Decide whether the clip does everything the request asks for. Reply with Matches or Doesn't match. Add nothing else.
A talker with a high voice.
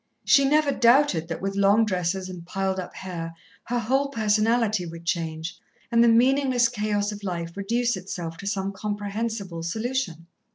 Matches